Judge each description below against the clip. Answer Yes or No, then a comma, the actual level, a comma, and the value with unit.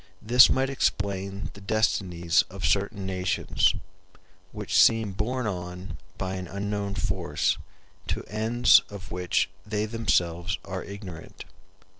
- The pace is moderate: No, slow, 120 wpm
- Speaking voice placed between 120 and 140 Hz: No, low, 100 Hz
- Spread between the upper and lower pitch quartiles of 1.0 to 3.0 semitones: Yes, narrow, 2.6 semitones